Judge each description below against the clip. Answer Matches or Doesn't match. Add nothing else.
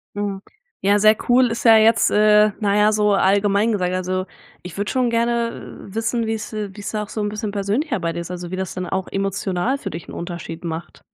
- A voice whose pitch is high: Matches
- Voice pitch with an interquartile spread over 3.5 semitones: Doesn't match